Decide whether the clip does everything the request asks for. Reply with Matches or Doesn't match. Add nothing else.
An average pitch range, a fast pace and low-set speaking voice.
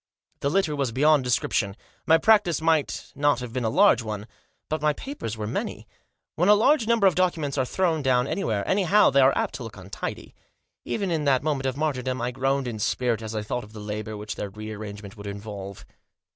Doesn't match